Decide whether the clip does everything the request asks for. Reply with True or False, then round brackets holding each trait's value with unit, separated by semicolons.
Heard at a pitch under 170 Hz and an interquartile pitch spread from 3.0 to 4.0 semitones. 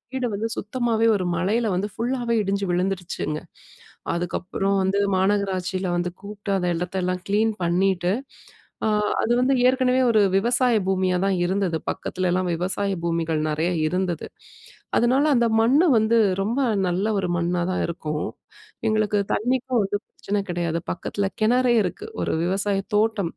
False (195 Hz; 3.7 semitones)